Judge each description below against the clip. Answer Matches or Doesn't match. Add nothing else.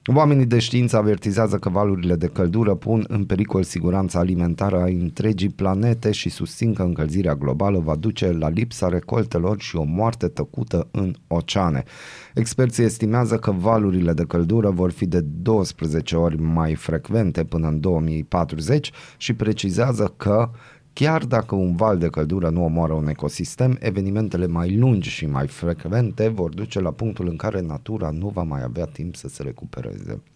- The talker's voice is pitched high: Doesn't match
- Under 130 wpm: Doesn't match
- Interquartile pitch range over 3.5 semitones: Matches